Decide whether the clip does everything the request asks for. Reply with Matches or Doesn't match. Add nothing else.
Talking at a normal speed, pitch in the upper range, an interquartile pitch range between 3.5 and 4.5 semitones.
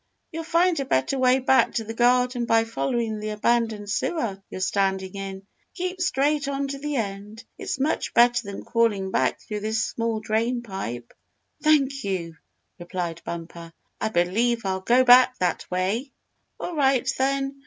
Doesn't match